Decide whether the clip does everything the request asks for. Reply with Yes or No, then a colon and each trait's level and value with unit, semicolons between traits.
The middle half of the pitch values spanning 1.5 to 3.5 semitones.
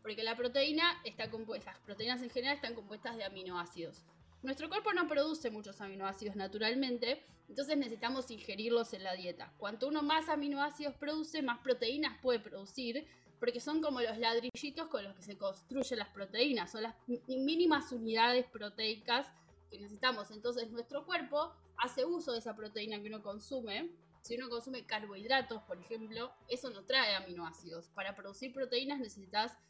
No: average, 4.1 semitones